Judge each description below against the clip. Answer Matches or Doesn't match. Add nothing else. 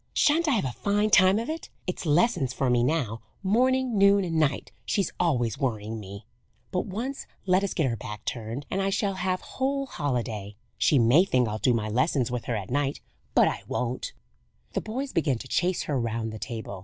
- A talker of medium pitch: Matches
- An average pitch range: Doesn't match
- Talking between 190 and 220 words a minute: Matches